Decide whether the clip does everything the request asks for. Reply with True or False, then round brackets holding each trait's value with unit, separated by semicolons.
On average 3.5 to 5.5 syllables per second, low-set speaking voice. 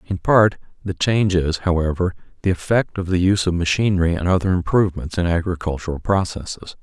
False (6.1 syllables/s; 90 Hz)